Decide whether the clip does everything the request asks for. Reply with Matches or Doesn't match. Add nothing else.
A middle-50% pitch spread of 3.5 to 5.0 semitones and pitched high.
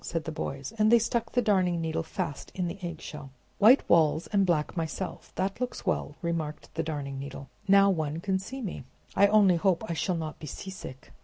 Doesn't match